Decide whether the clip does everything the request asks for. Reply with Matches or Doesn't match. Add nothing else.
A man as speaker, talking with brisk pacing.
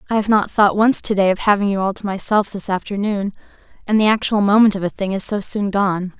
Doesn't match